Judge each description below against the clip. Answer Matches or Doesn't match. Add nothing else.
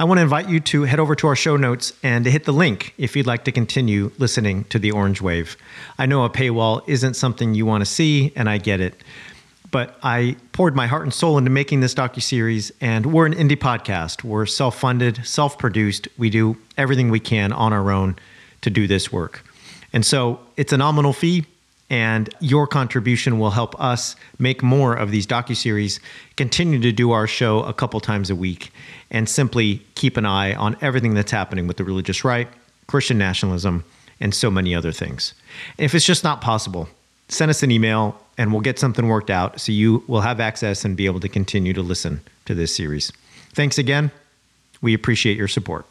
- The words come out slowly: Doesn't match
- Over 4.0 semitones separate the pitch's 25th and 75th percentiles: Matches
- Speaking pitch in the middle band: Doesn't match